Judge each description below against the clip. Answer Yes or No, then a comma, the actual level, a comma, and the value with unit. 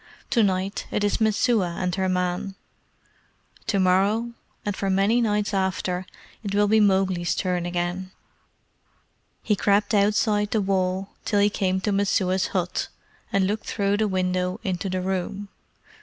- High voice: Yes, high, 195 Hz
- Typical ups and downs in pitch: No, narrow, 2.0 semitones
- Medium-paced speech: Yes, average, 155 wpm